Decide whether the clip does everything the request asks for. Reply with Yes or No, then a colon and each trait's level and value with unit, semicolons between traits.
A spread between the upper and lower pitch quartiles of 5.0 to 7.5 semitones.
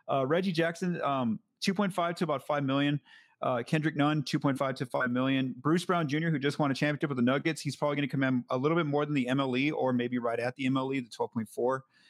No: average, 3.6 semitones